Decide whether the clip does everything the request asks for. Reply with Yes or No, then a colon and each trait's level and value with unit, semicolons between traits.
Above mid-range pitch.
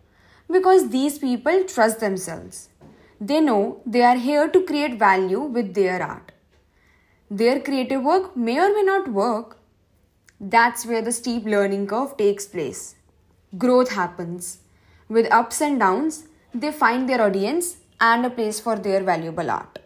Yes: high, 230 Hz